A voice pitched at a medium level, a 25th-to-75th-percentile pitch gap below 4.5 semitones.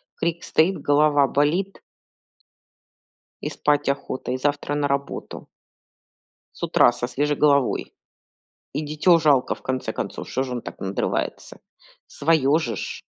Yes: medium, 145 Hz; narrow, 2.6 semitones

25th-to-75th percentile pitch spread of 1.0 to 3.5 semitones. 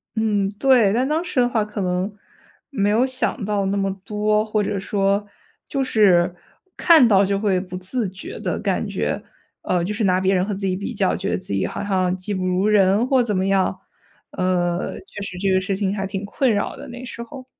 Yes: average, 2.7 semitones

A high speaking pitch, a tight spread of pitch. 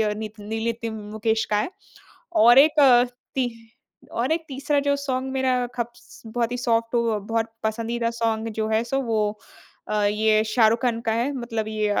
Yes: high, 230 Hz; narrow, 2.2 semitones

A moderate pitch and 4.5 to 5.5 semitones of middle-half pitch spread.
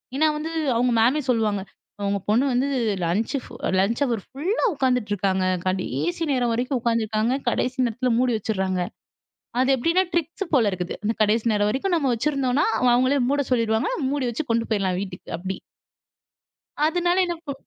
No: high, 240 Hz; average, 4.9 semitones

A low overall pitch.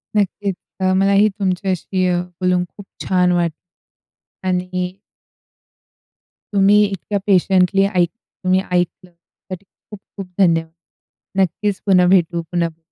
No: medium, 185 Hz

